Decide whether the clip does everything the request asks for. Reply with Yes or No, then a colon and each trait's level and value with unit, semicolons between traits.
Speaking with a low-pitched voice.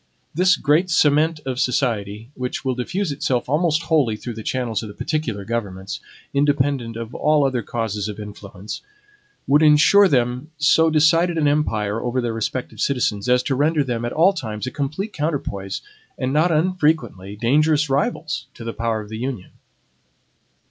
Yes: low, 130 Hz